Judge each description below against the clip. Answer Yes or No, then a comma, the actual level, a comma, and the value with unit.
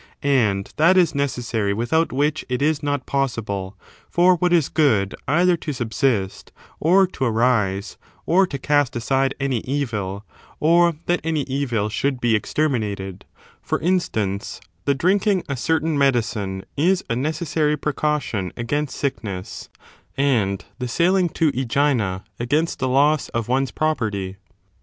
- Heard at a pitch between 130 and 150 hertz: Yes, low, 135 Hz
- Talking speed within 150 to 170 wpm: No, average, 140 wpm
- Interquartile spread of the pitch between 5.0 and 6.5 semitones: Yes, wide, 5.6 semitones